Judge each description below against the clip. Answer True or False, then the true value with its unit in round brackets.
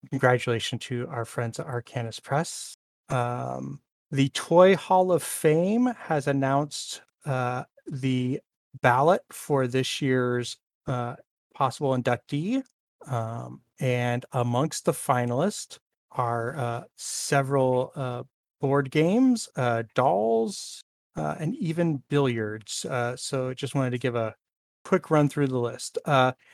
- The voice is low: True (130 Hz)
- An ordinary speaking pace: False (120 wpm)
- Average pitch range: True (3.7 semitones)